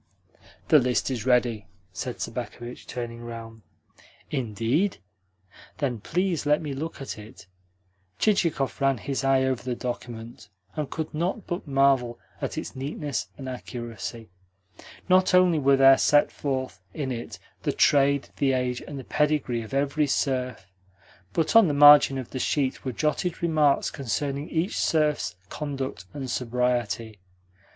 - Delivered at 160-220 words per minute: No, average, 145 wpm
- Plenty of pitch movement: No, average, 3.6 semitones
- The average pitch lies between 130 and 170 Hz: Yes, low, 135 Hz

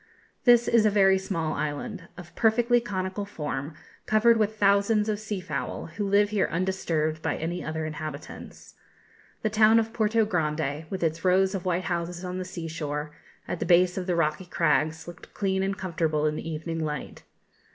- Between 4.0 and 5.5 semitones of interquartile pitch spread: Yes, average, 4.4 semitones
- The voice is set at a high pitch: No, medium, 180 Hz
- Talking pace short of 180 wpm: No, average, 185 wpm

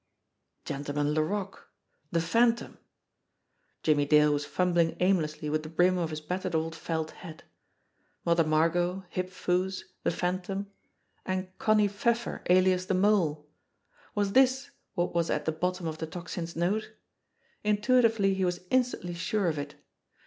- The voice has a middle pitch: Yes, medium, 180 Hz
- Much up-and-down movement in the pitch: No, average, 3.6 semitones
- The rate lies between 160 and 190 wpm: No, average, 150 wpm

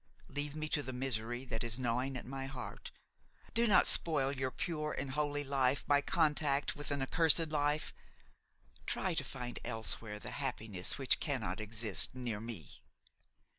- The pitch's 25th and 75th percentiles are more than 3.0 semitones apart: Yes, average, 3.7 semitones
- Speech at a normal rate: Yes, average, 165 wpm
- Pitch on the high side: No, low, 135 Hz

